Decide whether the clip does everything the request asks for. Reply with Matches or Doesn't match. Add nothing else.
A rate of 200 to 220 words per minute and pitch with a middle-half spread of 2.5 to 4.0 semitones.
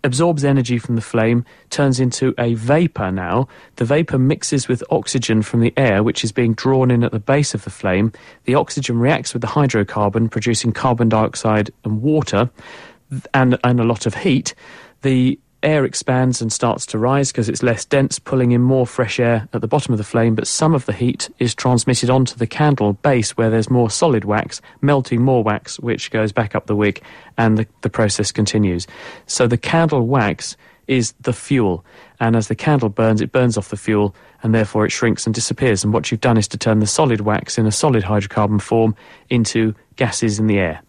Matches